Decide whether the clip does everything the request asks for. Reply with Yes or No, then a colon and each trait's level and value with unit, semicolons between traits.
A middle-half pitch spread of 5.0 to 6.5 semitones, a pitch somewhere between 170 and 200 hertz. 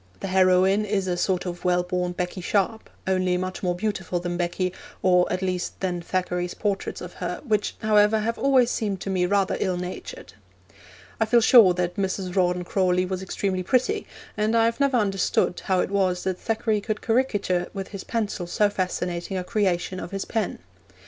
No: average, 2.8 semitones; high, 190 Hz